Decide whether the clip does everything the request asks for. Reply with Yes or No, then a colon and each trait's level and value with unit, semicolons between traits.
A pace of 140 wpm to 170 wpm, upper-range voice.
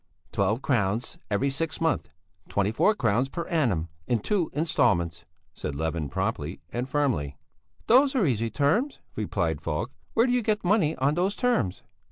No: average, 160 wpm; low, 130 Hz